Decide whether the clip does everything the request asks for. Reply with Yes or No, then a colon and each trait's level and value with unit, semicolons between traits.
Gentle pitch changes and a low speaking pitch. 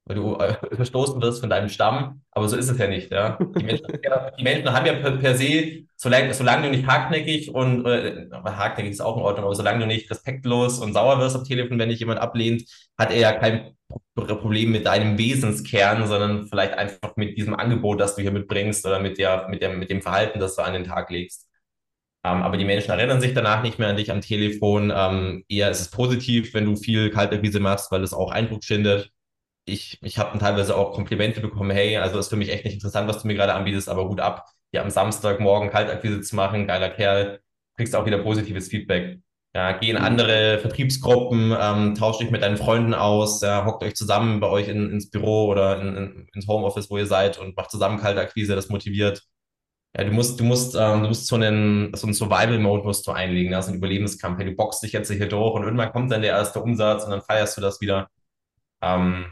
Yes: narrow, 2.2 semitones; low, 105 Hz